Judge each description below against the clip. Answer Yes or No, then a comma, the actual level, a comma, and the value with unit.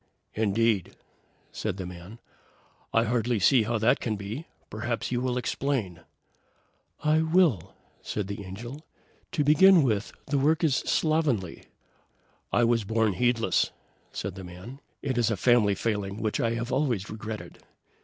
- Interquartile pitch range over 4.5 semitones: No, average, 4.2 semitones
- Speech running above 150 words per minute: No, average, 145 wpm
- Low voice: Yes, low, 115 Hz